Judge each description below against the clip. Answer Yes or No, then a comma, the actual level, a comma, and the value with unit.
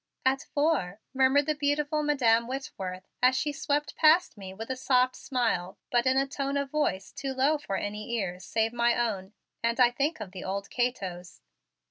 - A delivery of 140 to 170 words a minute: No, average, 185 wpm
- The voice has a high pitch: Yes, very high, 250 Hz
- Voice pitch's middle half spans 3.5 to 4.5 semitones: No, wide, 5.4 semitones